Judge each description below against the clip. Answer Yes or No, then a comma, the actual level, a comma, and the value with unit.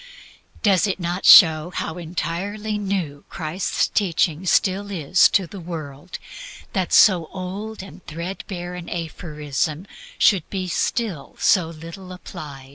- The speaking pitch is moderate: Yes, medium, 175 Hz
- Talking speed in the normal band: No, slow, 125 wpm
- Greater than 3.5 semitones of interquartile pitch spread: No, average, 3.2 semitones